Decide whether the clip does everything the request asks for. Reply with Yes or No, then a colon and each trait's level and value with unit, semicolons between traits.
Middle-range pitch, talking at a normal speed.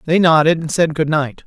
No: medium, 155 Hz; fast, 245 wpm